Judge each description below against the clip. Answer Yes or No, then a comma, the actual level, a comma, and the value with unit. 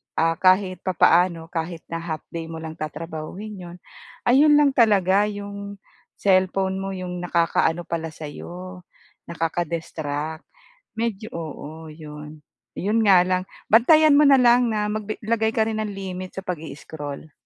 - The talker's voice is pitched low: No, medium, 185 Hz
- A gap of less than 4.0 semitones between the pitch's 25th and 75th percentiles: No, average, 4.3 semitones